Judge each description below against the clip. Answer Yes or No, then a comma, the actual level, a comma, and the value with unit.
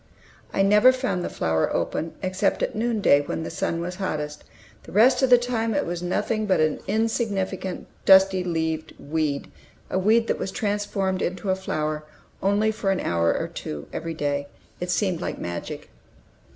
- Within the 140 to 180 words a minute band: Yes, average, 175 wpm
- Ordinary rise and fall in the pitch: Yes, average, 4.7 semitones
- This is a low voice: No, high, 190 Hz